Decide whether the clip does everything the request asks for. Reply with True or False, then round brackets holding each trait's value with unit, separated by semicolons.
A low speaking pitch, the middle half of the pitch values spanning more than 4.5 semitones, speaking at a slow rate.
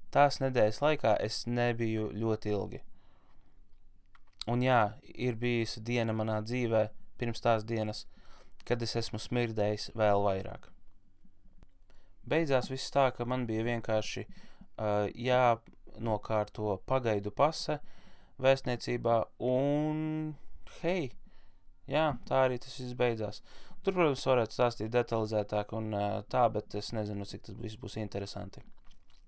False (115 Hz; 3.3 semitones; 115 wpm)